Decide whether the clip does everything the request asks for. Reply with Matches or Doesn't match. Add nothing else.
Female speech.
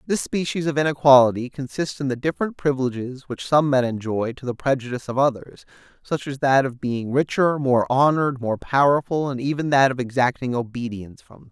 Doesn't match